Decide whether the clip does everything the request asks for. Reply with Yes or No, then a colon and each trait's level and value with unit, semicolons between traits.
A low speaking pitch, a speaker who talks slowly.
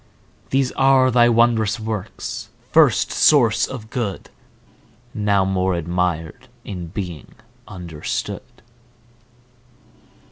Yes: low, 105 Hz; slow, 85 wpm